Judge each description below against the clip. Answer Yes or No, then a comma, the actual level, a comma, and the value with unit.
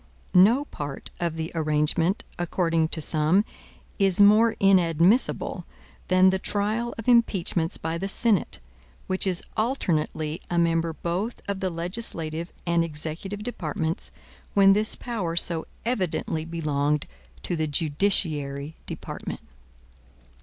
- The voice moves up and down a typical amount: Yes, average, 3.9 semitones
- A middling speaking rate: No, slow, 120 wpm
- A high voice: No, medium, 170 Hz